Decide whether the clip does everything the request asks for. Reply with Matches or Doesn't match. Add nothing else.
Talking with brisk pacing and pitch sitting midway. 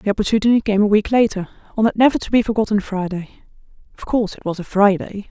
Doesn't match